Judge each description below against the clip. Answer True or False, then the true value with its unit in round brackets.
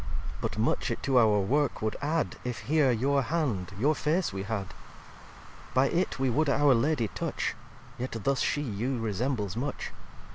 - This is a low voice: True (130 Hz)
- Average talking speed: True (175 wpm)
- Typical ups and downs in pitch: True (4.7 semitones)